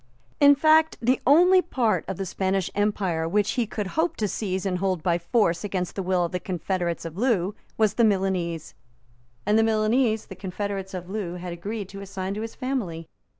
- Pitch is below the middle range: No, high, 195 Hz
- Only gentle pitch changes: No, average, 3.5 semitones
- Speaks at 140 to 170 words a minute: No, average, 195 wpm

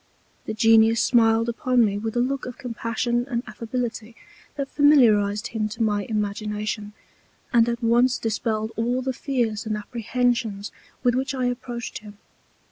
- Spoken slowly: No, average, 150 wpm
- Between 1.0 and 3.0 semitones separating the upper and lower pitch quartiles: Yes, narrow, 2.4 semitones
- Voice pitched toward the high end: Yes, high, 230 Hz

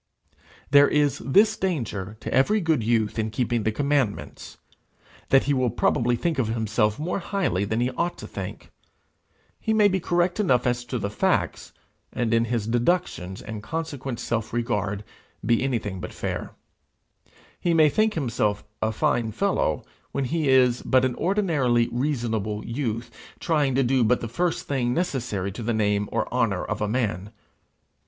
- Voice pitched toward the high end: No, low, 120 Hz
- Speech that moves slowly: No, average, 165 wpm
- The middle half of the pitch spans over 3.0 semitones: Yes, average, 5.1 semitones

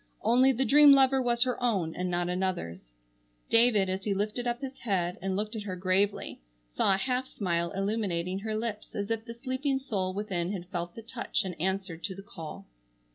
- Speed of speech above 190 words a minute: Yes, average, 200 wpm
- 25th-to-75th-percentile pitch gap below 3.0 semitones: No, average, 4.4 semitones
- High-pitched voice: Yes, high, 200 Hz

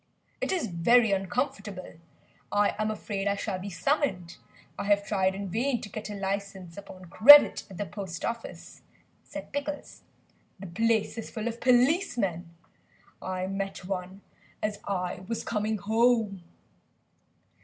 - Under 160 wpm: Yes, average, 145 wpm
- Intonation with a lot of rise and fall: No, average, 3.4 semitones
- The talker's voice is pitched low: No, high, 205 Hz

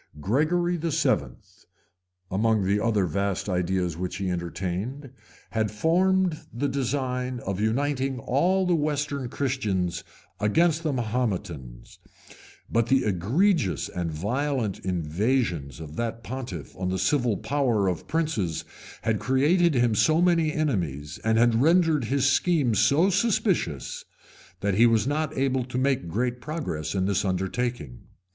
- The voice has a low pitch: Yes, low, 120 Hz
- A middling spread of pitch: No, wide, 7.3 semitones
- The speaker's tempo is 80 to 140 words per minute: Yes, slow, 135 wpm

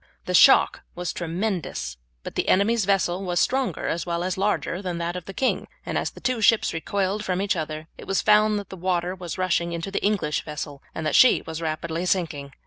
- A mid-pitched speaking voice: Yes, medium, 180 Hz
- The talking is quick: Yes, fast, 220 wpm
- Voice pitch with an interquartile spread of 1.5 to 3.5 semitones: Yes, average, 3.1 semitones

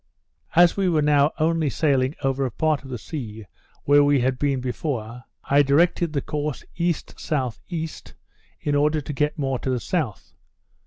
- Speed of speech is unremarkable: Yes, average, 165 wpm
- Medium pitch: Yes, medium, 145 Hz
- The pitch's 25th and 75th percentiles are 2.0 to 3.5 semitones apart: Yes, average, 3.1 semitones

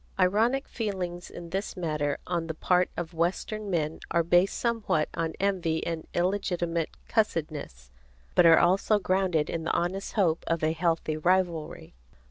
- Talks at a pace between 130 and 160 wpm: Yes, average, 150 wpm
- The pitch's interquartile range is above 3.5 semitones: No, average, 2.8 semitones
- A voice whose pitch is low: No, medium, 175 Hz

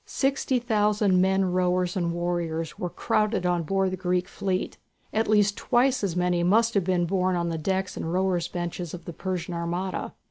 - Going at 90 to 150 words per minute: No, average, 185 wpm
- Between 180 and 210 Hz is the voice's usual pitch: Yes, medium, 185 Hz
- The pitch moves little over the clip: Yes, narrow, 2.3 semitones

